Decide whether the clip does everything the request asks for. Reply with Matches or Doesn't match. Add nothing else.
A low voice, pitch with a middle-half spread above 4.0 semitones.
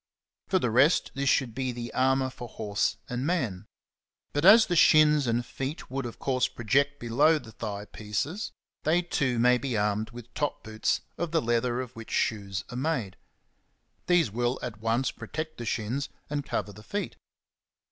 Matches